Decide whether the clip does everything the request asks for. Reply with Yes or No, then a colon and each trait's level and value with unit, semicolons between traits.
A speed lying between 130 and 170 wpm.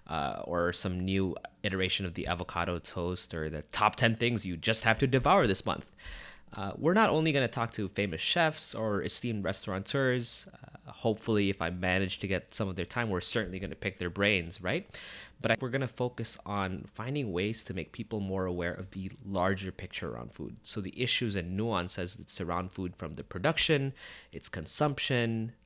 No: average, 195 wpm